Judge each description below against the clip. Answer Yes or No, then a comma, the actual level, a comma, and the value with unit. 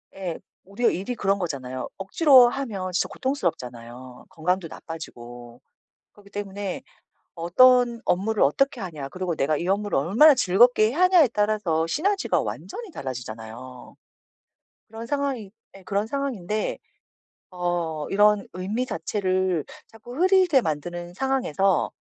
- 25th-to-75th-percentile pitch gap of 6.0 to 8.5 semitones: Yes, wide, 6.7 semitones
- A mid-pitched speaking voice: No, high, 195 Hz